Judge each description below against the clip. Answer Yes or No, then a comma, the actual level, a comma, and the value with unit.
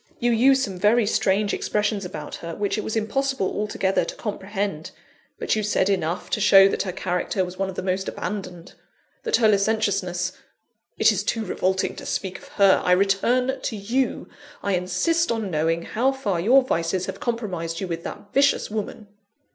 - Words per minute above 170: Yes, average, 185 wpm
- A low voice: No, high, 200 Hz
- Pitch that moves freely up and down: No, average, 3.2 semitones